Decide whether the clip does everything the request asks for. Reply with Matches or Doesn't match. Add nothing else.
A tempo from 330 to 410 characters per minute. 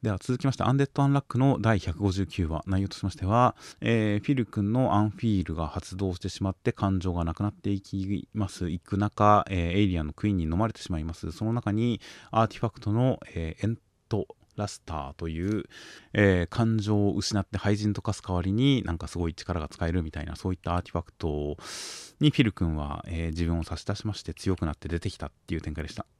Doesn't match